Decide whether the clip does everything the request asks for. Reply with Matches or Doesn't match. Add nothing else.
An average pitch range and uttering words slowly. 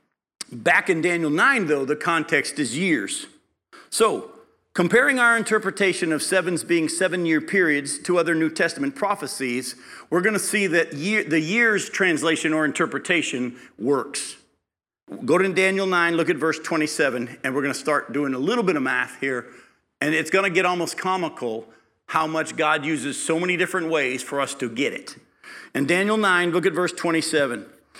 Doesn't match